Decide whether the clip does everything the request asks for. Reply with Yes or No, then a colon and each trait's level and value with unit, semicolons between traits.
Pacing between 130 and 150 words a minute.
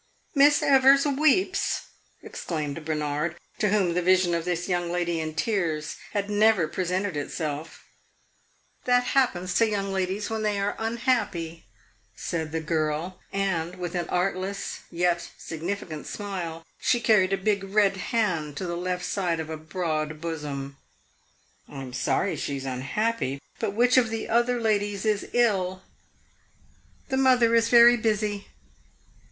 Yes: average, 145 wpm